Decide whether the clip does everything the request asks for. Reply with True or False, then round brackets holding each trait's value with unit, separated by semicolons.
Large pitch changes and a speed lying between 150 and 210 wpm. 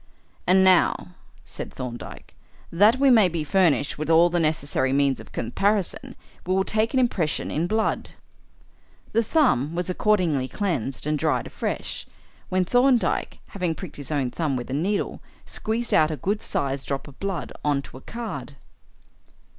True (6.3 semitones; 160 wpm)